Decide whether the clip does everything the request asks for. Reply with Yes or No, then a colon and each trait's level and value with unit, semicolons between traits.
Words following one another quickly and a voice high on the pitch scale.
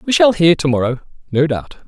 No: fast, 225 wpm; medium, 165 Hz